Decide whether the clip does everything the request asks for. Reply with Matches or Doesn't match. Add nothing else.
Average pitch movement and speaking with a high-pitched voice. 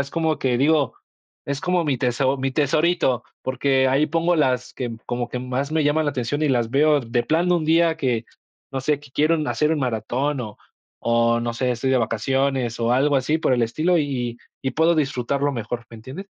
Doesn't match